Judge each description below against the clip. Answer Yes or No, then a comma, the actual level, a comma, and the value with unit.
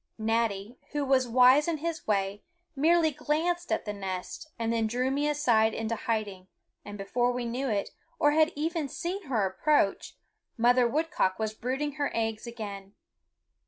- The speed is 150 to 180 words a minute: Yes, average, 160 wpm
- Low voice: No, high, 245 Hz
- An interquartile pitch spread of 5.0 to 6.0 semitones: Yes, wide, 5.4 semitones